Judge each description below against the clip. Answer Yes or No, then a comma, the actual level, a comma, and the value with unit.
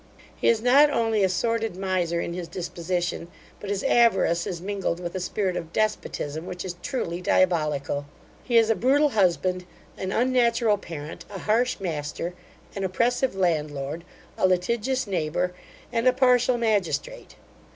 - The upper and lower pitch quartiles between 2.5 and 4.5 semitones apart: No, average, 5.3 semitones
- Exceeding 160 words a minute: No, average, 150 wpm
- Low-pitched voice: No, high, 190 Hz